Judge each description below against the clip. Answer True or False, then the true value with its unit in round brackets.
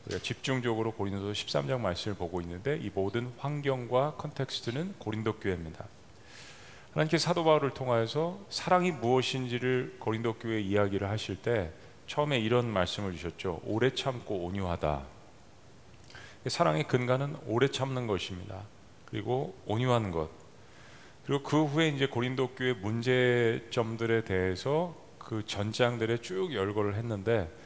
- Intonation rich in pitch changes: False (4.5 semitones)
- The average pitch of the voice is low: True (115 Hz)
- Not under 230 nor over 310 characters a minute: False (320 characters per minute)